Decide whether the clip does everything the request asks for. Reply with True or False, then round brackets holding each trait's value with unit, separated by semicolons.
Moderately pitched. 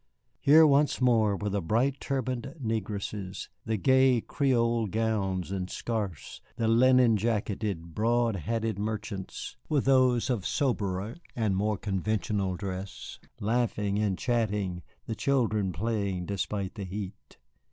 False (110 Hz)